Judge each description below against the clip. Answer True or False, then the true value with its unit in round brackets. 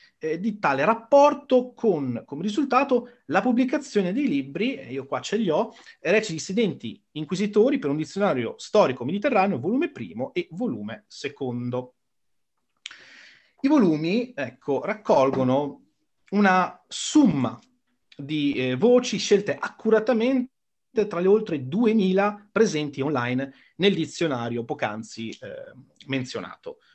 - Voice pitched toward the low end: False (205 Hz)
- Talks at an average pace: False (110 wpm)